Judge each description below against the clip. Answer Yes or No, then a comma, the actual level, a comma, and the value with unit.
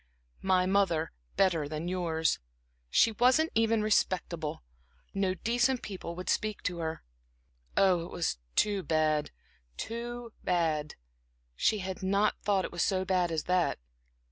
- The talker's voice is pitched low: No, medium, 185 Hz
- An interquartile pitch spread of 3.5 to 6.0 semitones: Yes, average, 4.0 semitones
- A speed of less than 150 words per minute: Yes, average, 140 wpm